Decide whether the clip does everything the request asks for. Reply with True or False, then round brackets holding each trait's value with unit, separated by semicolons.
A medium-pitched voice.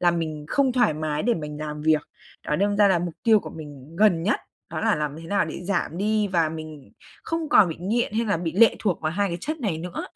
True (175 Hz)